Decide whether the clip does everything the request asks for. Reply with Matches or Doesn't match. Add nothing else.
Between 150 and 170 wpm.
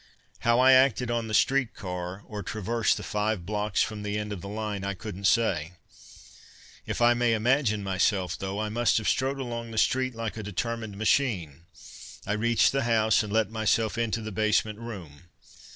Doesn't match